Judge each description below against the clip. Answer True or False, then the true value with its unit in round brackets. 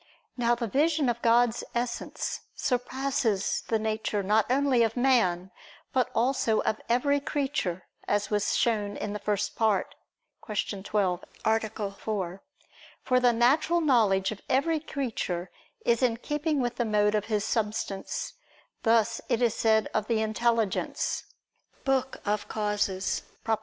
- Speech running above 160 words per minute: False (140 wpm)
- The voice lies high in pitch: True (225 Hz)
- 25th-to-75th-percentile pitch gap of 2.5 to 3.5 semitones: True (3.2 semitones)